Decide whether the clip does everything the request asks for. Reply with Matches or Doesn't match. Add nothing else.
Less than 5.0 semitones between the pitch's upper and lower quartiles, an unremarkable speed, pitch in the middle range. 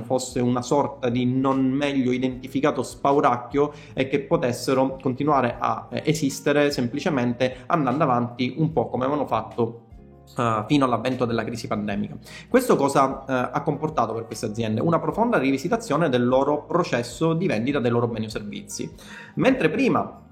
Doesn't match